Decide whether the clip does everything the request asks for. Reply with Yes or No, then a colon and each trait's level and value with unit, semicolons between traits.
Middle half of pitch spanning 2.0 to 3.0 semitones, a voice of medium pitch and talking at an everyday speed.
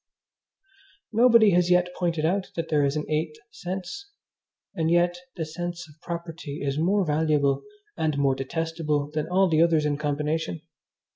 Yes: average, 2.7 semitones; medium, 160 Hz; average, 155 wpm